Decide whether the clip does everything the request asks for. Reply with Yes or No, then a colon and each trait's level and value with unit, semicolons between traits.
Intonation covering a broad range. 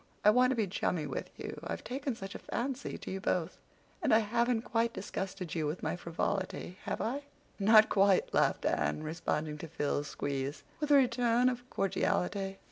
Yes: wide, 6.1 semitones